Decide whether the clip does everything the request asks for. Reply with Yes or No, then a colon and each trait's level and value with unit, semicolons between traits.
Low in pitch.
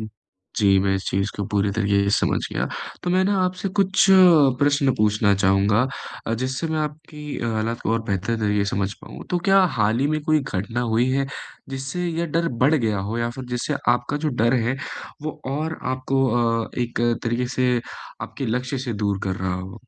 Yes: low, 120 Hz